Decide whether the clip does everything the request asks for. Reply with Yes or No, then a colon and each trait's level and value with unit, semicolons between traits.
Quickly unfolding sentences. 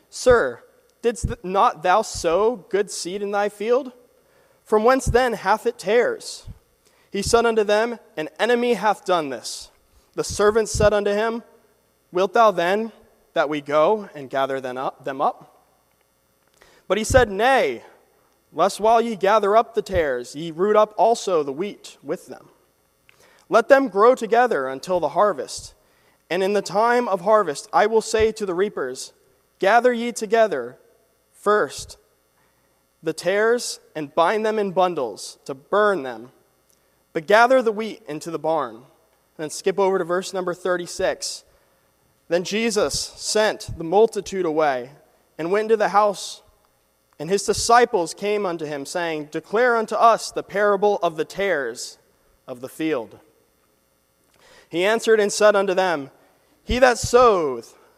No: average, 150 wpm